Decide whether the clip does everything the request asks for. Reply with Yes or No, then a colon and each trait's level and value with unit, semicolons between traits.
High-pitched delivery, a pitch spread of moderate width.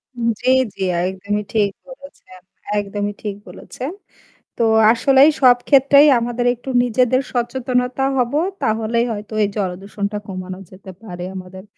Yes: high, 225 Hz; average, 4.1 semitones